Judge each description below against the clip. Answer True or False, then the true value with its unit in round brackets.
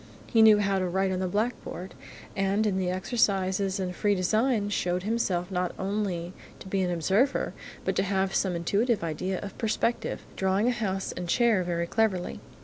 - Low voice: False (190 Hz)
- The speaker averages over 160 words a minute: True (185 wpm)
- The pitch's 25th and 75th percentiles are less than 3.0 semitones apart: True (2.6 semitones)